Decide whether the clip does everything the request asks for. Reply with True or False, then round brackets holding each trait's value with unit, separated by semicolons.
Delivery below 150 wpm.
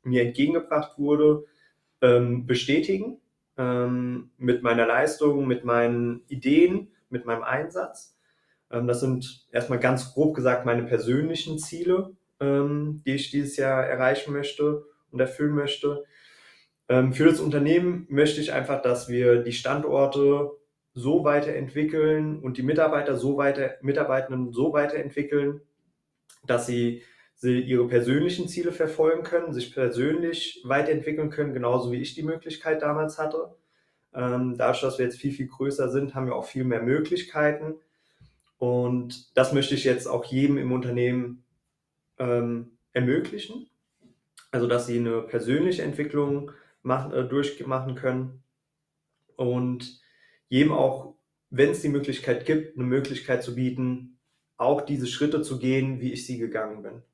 True (130 wpm)